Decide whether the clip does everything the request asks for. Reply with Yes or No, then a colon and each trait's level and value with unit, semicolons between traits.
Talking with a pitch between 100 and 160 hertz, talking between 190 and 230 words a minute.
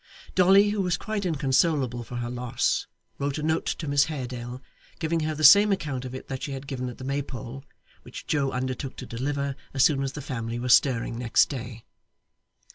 Yes: low, 135 Hz; average, 200 wpm